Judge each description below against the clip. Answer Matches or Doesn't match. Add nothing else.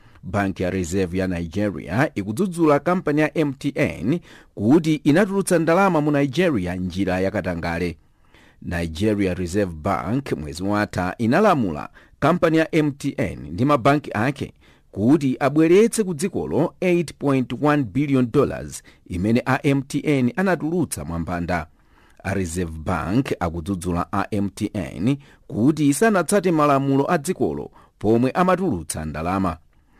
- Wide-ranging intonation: Matches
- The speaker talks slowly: Matches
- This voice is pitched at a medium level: Doesn't match